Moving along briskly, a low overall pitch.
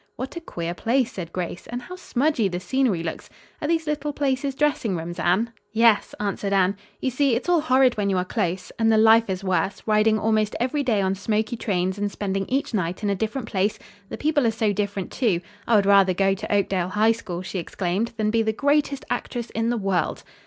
No: fast, 220 wpm; high, 215 Hz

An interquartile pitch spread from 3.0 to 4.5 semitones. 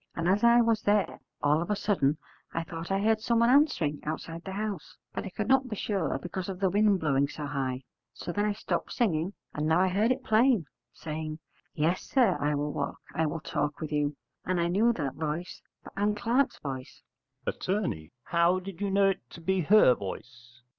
No: wide, 5.6 semitones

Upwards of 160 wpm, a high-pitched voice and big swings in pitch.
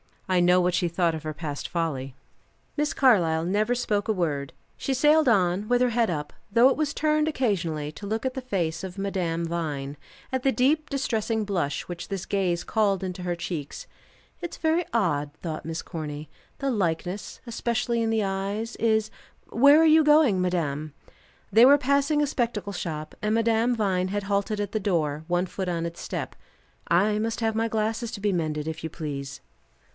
Yes: average, 190 wpm; high, 200 Hz; wide, 5.7 semitones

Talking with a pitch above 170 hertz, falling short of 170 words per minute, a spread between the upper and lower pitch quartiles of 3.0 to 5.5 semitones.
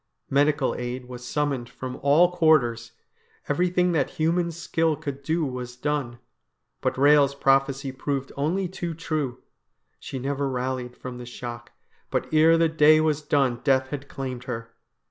No: medium, 140 Hz; average, 150 wpm; average, 3.6 semitones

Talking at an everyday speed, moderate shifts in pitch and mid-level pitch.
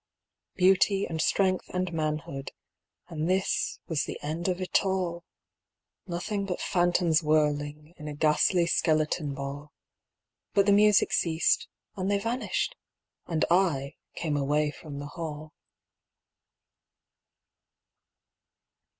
No: slow, 115 wpm; average, 3.6 semitones; medium, 165 Hz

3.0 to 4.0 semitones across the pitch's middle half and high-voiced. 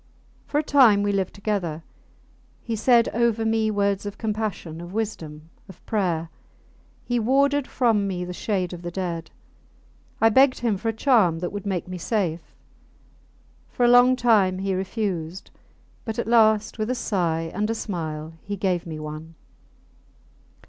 No: average, 4.4 semitones; high, 200 Hz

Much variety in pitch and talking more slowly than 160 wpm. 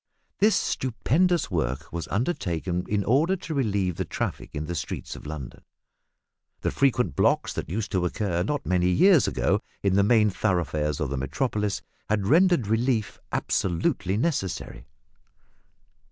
Yes: wide, 7.0 semitones; average, 145 wpm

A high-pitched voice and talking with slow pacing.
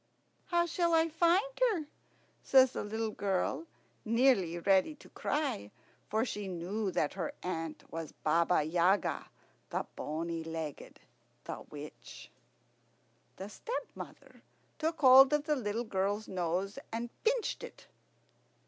Yes: high, 205 Hz; slow, 125 wpm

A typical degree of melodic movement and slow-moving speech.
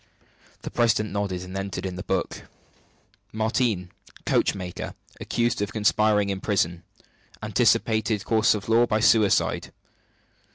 No: narrow, 2.3 semitones; slow, 120 wpm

